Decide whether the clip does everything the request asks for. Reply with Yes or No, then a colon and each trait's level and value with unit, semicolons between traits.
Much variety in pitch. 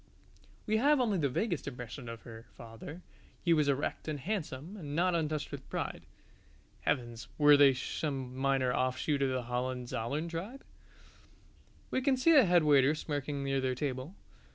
No: average, 4.8 semitones